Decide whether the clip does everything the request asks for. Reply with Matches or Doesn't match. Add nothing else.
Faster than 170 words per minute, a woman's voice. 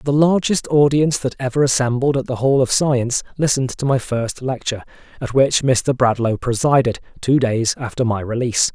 Doesn't match